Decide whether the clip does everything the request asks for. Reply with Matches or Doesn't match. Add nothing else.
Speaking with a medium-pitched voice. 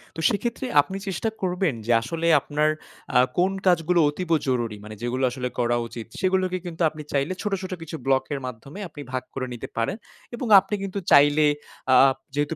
Matches